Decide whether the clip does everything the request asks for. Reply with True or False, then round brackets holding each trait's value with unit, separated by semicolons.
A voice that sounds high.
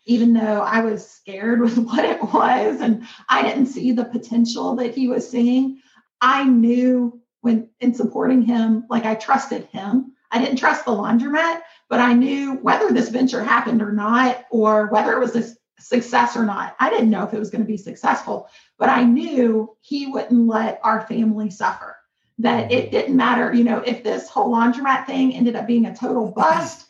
True (240 Hz)